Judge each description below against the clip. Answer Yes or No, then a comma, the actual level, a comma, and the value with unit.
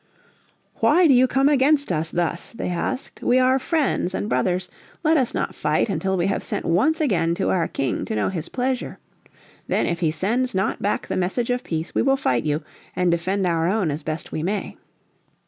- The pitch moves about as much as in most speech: No, wide, 7.3 semitones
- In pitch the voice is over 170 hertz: Yes, high, 190 Hz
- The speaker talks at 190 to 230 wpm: Yes, fast, 205 wpm